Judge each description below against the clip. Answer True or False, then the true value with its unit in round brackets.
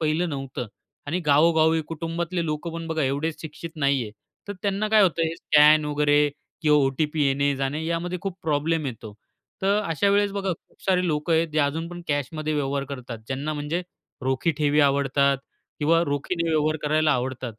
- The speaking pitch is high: False (155 Hz)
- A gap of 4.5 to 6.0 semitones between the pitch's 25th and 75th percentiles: False (2.9 semitones)